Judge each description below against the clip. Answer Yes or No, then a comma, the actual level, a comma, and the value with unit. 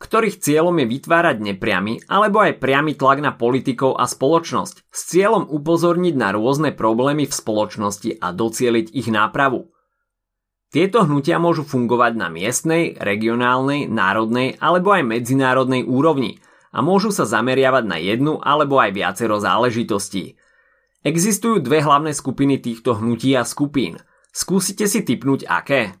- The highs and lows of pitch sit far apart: Yes, wide, 6.0 semitones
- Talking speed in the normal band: Yes, average, 135 wpm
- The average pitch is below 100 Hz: No, low, 135 Hz